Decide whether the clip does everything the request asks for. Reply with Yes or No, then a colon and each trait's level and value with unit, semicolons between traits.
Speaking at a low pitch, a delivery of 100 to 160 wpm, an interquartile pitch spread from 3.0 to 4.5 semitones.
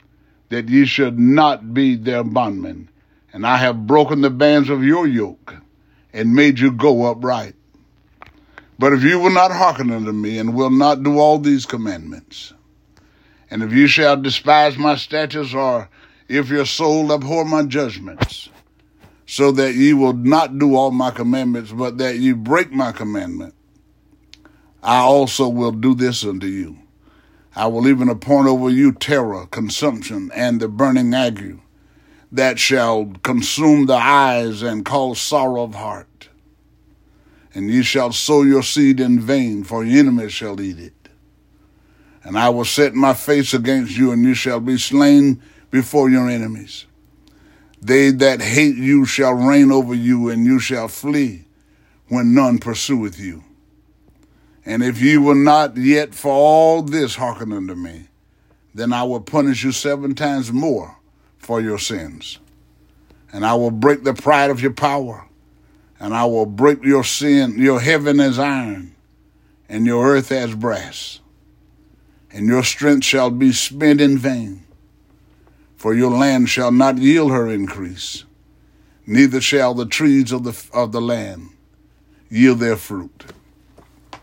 Yes: low, 130 Hz; average, 155 wpm; average, 3.3 semitones